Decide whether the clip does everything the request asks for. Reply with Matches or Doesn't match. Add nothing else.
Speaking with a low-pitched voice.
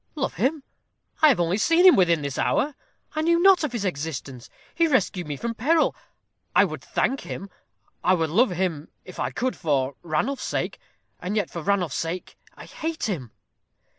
Doesn't match